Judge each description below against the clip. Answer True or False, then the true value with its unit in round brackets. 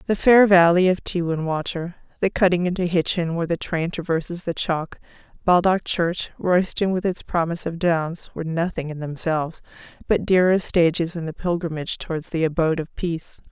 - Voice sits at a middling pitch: True (170 Hz)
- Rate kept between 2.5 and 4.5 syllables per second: False (5.4 syllables/s)